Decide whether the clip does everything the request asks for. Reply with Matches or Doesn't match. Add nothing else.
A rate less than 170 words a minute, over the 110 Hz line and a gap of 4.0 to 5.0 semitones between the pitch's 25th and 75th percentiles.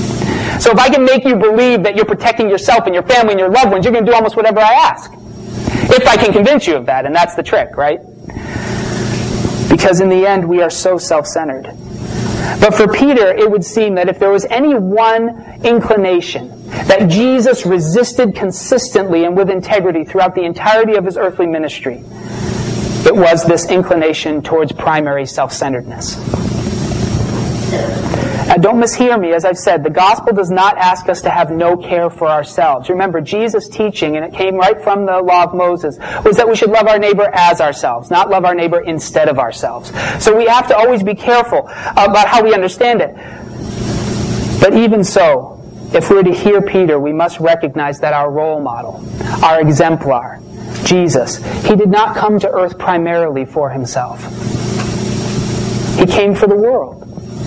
Doesn't match